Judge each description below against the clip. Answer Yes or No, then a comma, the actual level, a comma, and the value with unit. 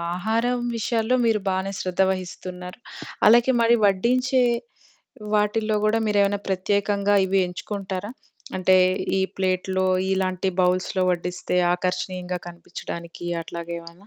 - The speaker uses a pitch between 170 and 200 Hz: Yes, high, 190 Hz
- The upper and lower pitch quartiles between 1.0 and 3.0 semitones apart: Yes, narrow, 2.6 semitones